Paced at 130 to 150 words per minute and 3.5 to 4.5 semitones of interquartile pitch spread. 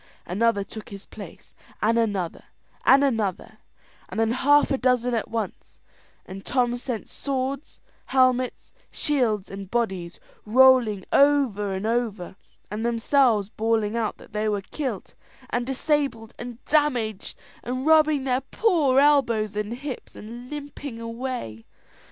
Yes: slow, 135 wpm; average, 3.9 semitones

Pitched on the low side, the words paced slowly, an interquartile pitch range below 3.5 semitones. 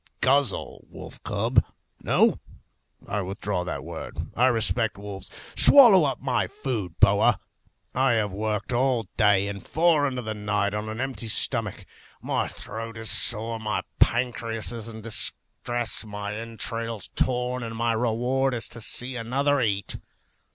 No: low, 115 Hz; average, 145 wpm; average, 3.0 semitones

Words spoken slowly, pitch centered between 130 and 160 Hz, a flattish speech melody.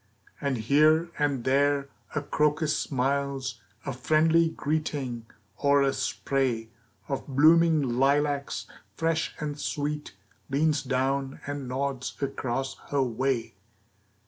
Yes: slow, 110 wpm; medium, 140 Hz; narrow, 2.1 semitones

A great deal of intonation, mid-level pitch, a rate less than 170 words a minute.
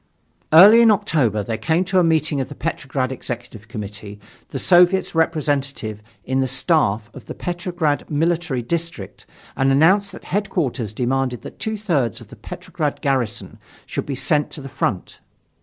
Yes: wide, 5.8 semitones; medium, 145 Hz; average, 160 wpm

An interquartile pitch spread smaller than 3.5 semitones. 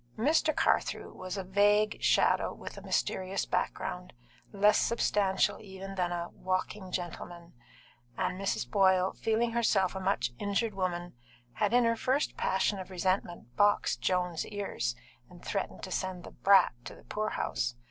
Yes: narrow, 2.5 semitones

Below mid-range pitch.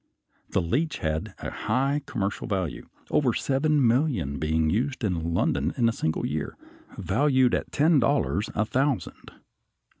Yes: low, 120 Hz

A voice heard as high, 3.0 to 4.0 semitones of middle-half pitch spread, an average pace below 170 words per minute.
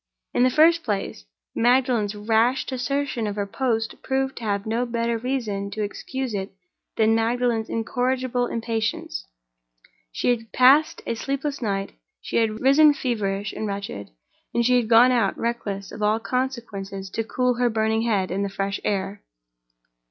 Yes: high, 225 Hz; average, 3.5 semitones; average, 160 wpm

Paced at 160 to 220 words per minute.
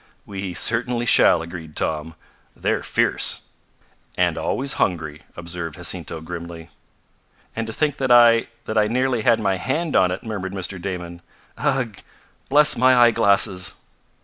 No: average, 140 wpm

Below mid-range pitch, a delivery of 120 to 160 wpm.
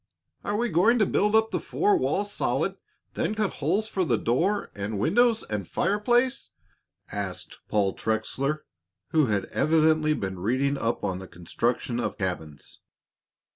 No: medium, 145 Hz; average, 155 wpm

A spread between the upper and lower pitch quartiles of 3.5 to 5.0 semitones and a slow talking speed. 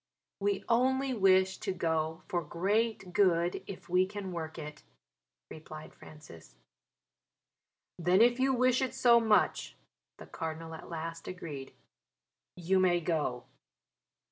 Yes: average, 4.4 semitones; slow, 125 wpm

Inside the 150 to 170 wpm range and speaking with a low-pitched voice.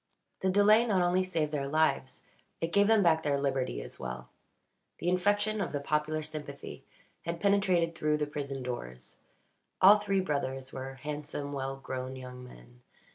No: average, 165 wpm; medium, 150 Hz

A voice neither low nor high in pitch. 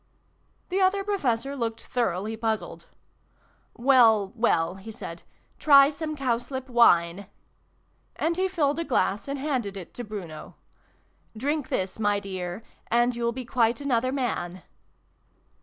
No: high, 235 Hz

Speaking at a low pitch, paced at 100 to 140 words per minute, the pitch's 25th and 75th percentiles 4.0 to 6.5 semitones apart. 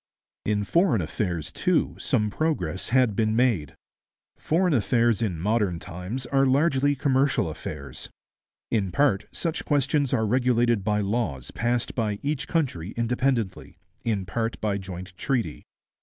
Yes: low, 115 Hz; slow, 135 wpm; wide, 5.4 semitones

